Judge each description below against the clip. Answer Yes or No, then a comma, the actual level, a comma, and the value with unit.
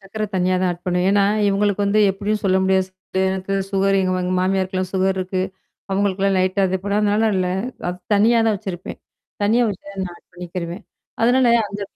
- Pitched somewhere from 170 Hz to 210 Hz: Yes, high, 190 Hz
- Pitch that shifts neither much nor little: No, narrow, 1.6 semitones